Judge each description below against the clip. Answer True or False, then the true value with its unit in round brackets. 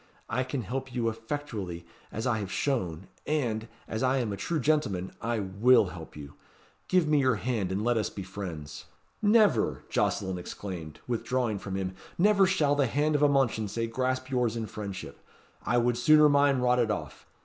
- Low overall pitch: True (120 Hz)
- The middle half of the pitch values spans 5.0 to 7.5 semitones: True (5.4 semitones)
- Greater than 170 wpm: True (180 wpm)